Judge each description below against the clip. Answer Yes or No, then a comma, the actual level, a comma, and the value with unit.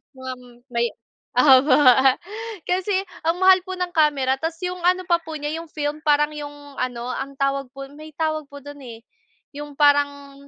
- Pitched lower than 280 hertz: No, very high, 290 Hz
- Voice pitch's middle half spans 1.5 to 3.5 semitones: Yes, average, 2.9 semitones